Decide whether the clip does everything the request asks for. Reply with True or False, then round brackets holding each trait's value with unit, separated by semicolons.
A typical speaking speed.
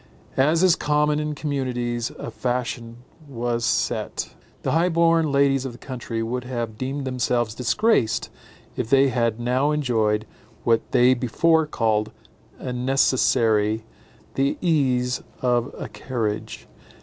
False (130 wpm)